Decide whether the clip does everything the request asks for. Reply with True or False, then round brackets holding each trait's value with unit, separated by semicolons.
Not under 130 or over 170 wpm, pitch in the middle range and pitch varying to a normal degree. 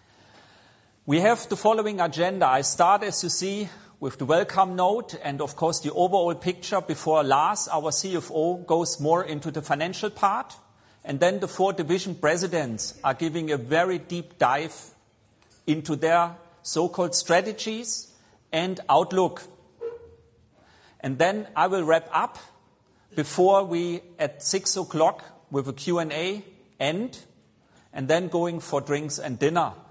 True (140 wpm; 170 Hz; 3.5 semitones)